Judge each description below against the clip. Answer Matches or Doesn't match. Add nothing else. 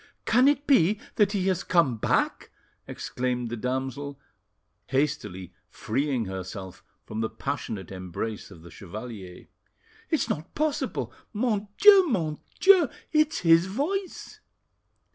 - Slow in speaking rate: Matches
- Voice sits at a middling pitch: Matches